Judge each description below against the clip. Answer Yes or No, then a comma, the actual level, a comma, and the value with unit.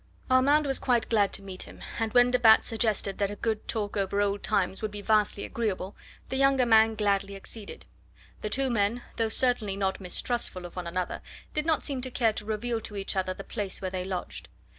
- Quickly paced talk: Yes, fast, 215 wpm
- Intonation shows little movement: No, average, 3.5 semitones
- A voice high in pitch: Yes, high, 215 Hz